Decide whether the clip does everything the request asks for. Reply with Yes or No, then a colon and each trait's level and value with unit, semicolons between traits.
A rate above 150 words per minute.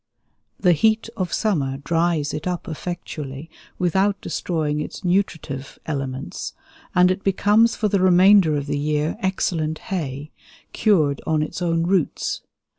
No: slow, 135 wpm